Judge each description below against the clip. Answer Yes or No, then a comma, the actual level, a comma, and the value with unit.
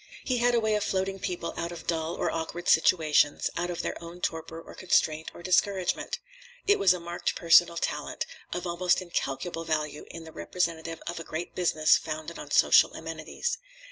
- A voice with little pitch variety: Yes, narrow, 2.0 semitones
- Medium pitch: Yes, medium, 170 Hz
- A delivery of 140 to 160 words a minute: No, average, 185 wpm